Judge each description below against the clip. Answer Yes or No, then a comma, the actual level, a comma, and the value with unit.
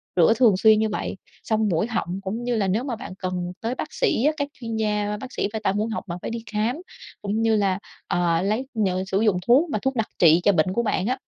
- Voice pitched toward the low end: No, high, 215 Hz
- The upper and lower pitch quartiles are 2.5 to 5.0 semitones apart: Yes, average, 3.5 semitones